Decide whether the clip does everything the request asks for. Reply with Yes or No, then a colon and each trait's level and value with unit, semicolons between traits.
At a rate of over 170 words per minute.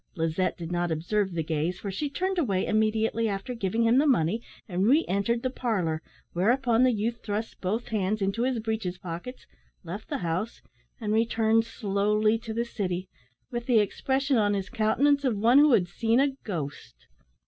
Yes: average, 180 wpm